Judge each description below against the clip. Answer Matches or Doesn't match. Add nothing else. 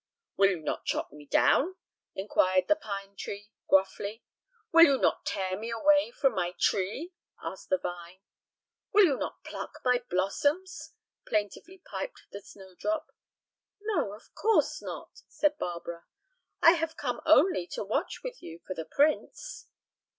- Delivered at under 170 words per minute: Matches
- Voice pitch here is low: Doesn't match